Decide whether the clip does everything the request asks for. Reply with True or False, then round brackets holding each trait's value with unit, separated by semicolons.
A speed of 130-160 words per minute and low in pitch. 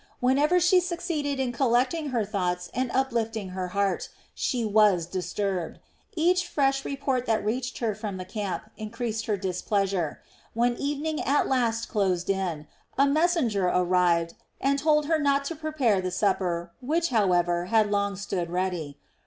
False (155 wpm; 220 Hz)